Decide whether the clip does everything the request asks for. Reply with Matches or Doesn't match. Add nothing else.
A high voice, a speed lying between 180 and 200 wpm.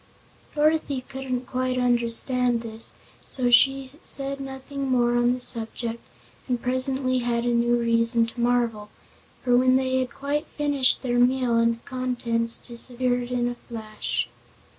Doesn't match